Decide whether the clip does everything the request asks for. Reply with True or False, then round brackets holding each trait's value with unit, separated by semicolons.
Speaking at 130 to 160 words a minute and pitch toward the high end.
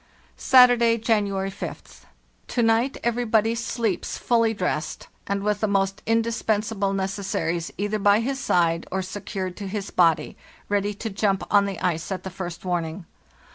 True (150 wpm; 200 Hz)